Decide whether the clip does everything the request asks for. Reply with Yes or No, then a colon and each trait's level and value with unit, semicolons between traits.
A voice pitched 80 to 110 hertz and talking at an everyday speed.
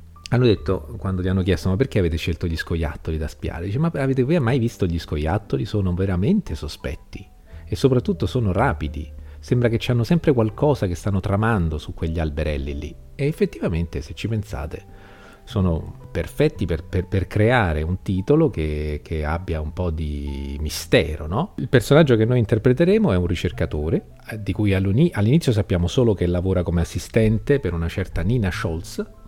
No: very low, 95 Hz; fast, 175 wpm